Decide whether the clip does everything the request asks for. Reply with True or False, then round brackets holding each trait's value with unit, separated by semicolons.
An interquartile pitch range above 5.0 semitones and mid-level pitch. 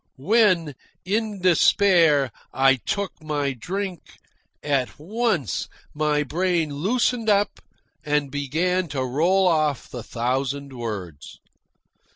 True (5.5 semitones; 155 Hz)